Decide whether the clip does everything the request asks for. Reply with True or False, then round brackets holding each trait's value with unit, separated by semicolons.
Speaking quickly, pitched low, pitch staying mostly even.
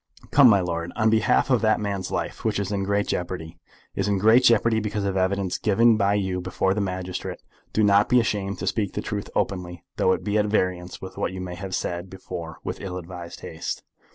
True (225 wpm; 100 Hz; 2.3 semitones)